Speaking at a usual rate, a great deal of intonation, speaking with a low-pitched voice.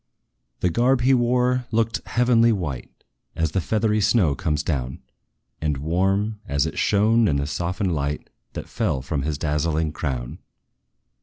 Yes: average, 150 wpm; wide, 7.2 semitones; very low, 90 Hz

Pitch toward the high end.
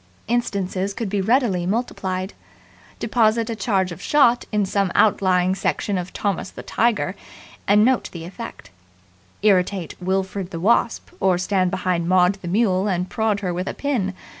Yes: high, 195 Hz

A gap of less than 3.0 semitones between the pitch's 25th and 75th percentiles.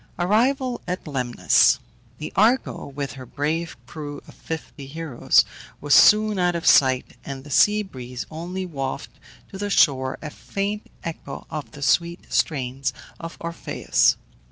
No: average, 5.3 semitones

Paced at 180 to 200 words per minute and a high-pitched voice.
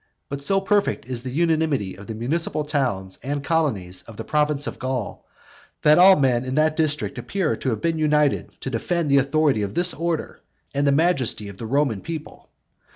No: average, 195 wpm; medium, 145 Hz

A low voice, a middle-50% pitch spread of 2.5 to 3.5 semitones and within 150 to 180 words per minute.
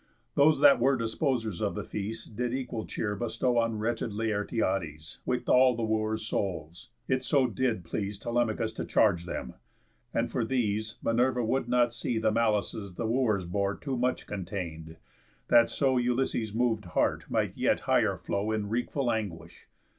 Yes: low, 110 Hz; average, 3.2 semitones; average, 160 wpm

